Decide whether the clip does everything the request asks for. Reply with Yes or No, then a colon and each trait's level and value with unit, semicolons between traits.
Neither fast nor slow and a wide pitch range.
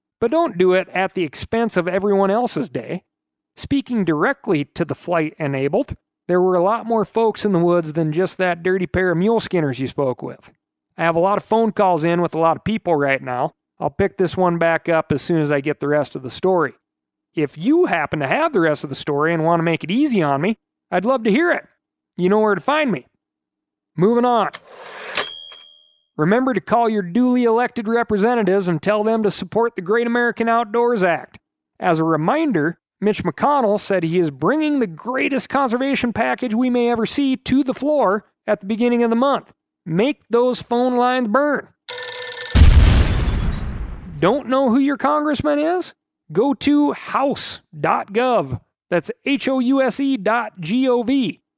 Yes: average, 195 wpm; wide, 6.3 semitones